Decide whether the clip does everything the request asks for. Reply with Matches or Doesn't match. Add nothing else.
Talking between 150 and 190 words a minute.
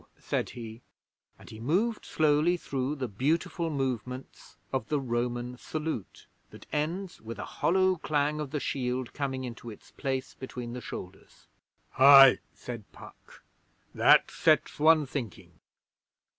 Doesn't match